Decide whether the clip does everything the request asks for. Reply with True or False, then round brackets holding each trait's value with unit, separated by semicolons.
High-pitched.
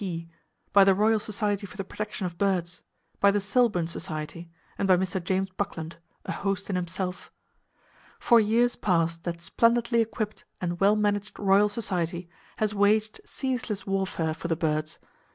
True (195 Hz)